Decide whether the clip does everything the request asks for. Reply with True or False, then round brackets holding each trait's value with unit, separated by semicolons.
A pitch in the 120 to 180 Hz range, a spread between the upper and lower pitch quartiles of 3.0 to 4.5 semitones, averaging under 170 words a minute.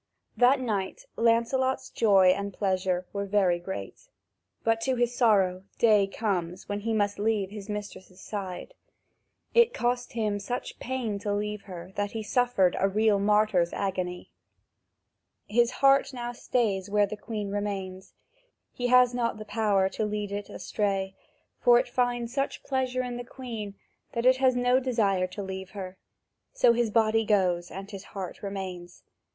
False (210 Hz; 3.8 semitones; 160 wpm)